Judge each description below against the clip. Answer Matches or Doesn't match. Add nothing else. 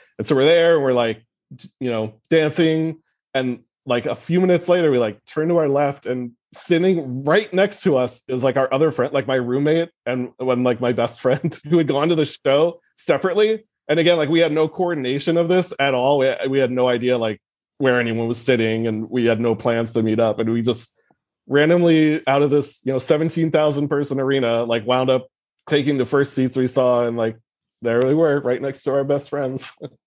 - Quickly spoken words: Matches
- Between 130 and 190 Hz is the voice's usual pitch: Matches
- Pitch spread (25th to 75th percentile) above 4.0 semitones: Matches